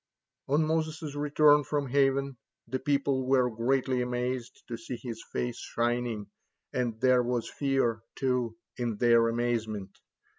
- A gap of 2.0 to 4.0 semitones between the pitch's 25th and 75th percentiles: Yes, average, 2.7 semitones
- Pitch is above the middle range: No, low, 125 Hz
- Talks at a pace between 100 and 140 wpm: Yes, slow, 135 wpm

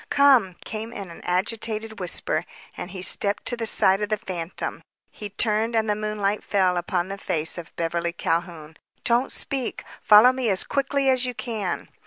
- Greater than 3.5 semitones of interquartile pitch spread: Yes, average, 4.1 semitones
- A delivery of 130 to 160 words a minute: No, average, 180 wpm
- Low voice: No, high, 210 Hz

